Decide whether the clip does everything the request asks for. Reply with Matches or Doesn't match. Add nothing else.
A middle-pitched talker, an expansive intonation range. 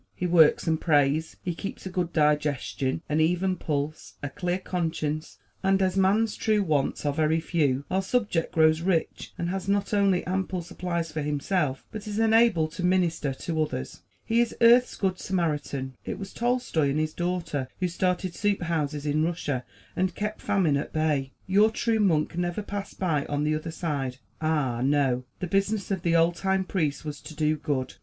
Doesn't match